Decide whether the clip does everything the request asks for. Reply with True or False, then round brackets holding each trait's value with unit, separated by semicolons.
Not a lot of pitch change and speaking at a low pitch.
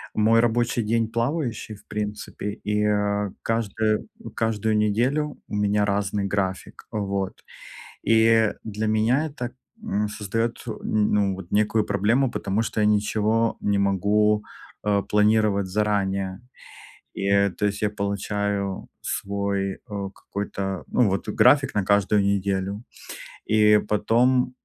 True (1.8 semitones; 105 Hz)